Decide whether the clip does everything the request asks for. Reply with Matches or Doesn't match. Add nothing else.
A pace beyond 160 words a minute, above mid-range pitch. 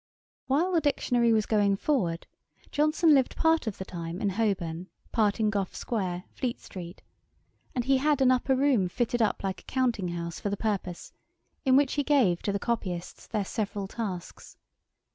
Matches